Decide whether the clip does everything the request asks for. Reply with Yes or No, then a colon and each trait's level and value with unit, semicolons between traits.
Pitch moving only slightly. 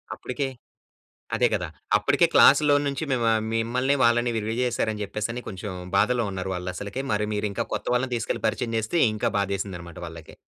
No: average, 3.8 semitones